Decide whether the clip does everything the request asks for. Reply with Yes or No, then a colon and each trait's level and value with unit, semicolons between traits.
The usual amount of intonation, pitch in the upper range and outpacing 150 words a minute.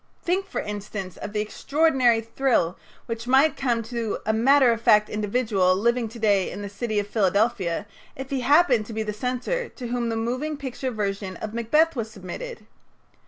Yes: average, 3.7 semitones; high, 230 Hz; average, 185 wpm